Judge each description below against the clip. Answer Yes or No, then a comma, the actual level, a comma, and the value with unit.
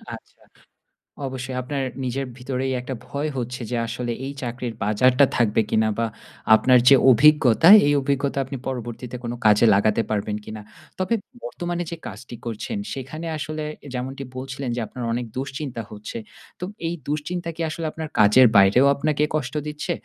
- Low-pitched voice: Yes, low, 130 Hz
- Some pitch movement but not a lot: Yes, average, 3.5 semitones